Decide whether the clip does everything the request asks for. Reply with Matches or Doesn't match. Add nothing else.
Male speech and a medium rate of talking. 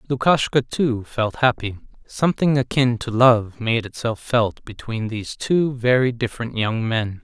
Matches